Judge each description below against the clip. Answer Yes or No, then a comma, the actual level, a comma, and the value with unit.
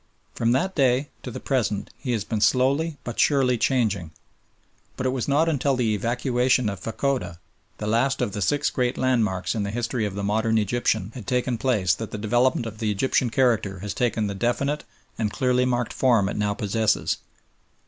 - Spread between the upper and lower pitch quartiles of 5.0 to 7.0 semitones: No, average, 3.6 semitones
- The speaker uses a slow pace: No, average, 190 wpm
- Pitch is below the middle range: Yes, low, 120 Hz